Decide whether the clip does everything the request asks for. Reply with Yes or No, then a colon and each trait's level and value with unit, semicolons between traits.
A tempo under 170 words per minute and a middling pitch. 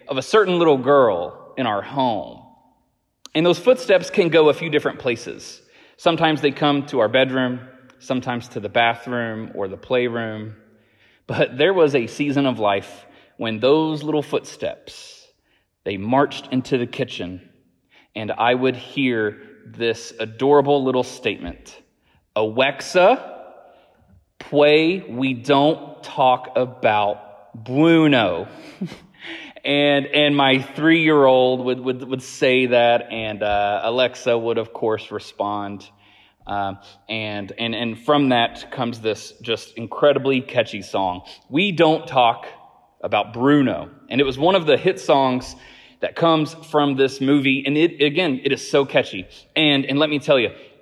No: average, 145 wpm; low, 130 Hz